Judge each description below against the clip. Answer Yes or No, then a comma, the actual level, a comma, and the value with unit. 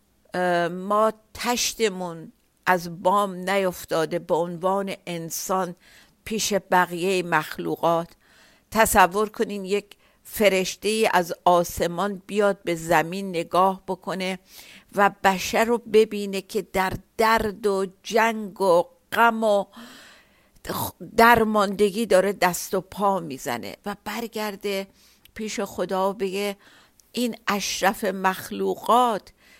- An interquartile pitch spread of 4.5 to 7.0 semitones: No, narrow, 2.6 semitones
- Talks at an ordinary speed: No, slow, 95 wpm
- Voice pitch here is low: No, high, 195 Hz